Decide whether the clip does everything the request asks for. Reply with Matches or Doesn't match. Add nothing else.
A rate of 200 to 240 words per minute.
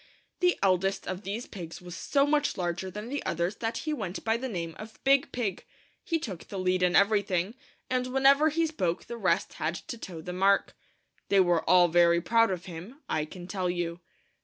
Matches